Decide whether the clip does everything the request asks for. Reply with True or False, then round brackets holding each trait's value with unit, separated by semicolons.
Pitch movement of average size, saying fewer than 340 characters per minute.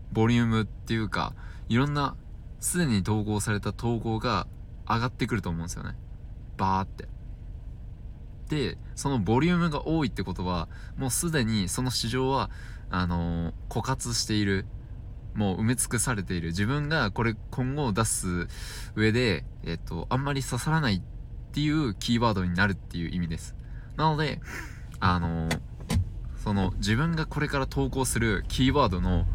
True (4.7 semitones; 320 characters per minute)